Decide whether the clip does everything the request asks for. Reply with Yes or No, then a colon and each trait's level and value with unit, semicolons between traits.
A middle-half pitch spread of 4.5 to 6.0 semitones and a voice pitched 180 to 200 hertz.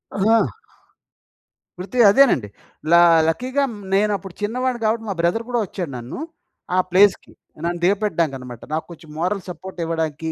Yes: average, 5.3 semitones; high, 190 Hz